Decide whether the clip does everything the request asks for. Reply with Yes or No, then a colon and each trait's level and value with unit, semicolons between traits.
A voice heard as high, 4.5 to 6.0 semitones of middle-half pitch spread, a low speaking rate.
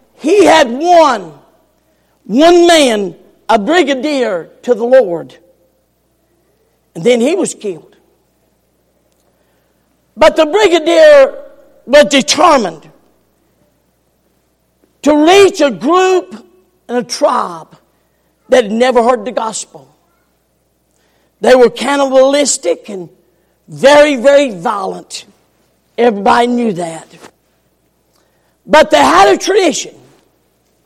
Yes: very high, 265 Hz; wide, 5.4 semitones; slow, 95 wpm